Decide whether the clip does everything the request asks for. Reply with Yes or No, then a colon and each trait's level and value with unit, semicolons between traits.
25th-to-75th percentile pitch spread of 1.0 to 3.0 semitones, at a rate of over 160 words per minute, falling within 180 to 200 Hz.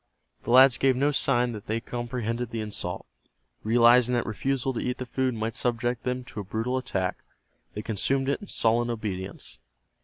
No: narrow, 2.4 semitones; average, 180 wpm; low, 120 Hz